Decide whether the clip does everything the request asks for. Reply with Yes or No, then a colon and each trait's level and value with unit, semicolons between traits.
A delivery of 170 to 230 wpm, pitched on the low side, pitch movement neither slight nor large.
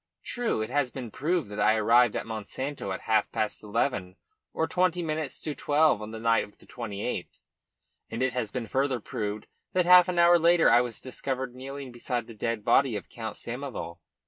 Yes: average, 200 wpm; low, 125 Hz; average, 4.8 semitones